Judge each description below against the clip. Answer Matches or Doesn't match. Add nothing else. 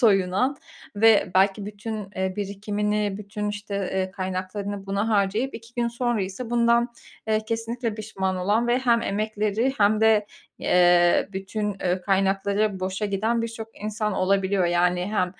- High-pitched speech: Matches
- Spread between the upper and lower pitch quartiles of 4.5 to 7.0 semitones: Doesn't match